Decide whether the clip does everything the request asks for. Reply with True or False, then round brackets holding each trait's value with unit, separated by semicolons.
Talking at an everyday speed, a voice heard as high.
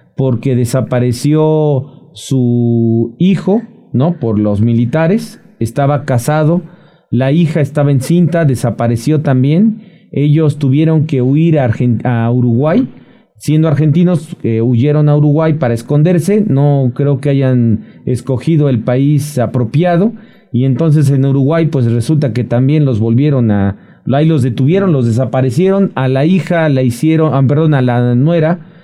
False (135 wpm; 140 Hz)